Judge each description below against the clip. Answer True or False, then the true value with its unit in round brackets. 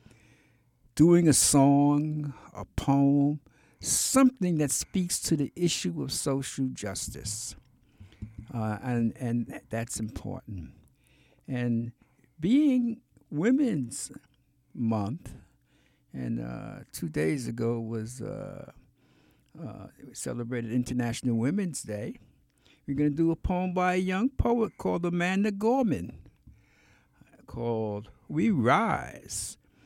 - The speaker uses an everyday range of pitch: False (6.6 semitones)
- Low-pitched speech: True (130 Hz)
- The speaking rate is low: True (105 wpm)